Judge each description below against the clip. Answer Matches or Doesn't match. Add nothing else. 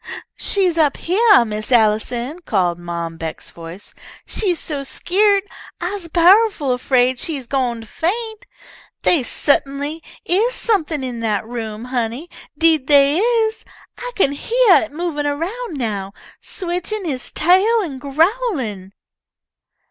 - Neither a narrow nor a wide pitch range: Doesn't match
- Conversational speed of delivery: Doesn't match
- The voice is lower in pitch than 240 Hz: Doesn't match